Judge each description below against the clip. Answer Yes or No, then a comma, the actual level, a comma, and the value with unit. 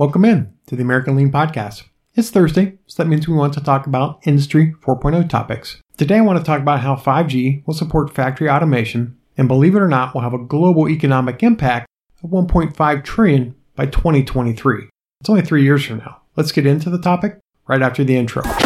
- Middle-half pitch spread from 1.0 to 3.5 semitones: No, average, 4.2 semitones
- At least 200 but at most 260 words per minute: Yes, fast, 205 wpm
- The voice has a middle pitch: Yes, medium, 145 Hz